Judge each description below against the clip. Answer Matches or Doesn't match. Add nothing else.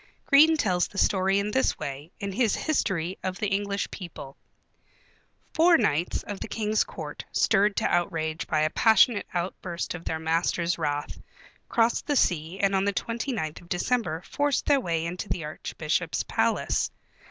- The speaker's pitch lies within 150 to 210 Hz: Matches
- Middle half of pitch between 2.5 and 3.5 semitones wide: Doesn't match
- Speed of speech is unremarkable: Matches